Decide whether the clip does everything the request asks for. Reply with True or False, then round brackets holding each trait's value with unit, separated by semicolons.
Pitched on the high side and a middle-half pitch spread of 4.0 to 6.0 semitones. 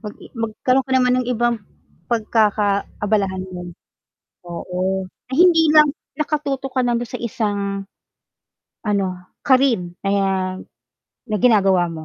True (215 Hz; 4.7 semitones)